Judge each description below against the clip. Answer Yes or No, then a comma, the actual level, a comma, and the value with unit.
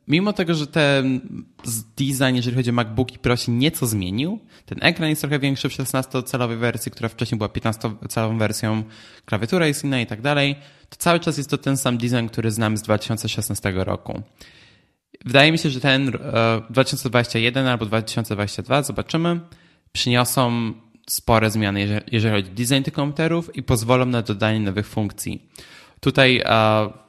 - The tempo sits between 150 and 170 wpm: Yes, average, 155 wpm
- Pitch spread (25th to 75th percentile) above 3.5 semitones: Yes, average, 4.0 semitones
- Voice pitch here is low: Yes, low, 125 Hz